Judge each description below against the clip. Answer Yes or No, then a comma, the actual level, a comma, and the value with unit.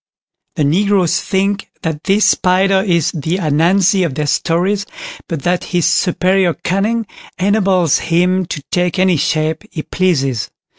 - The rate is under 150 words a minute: Yes, average, 140 wpm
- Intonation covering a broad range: No, average, 3.0 semitones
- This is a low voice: No, medium, 180 Hz